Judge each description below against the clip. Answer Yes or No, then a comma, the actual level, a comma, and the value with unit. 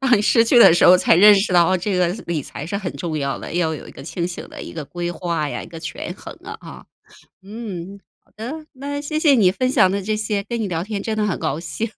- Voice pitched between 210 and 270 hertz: No, high, 195 Hz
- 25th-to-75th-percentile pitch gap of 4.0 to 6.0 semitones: Yes, average, 4.3 semitones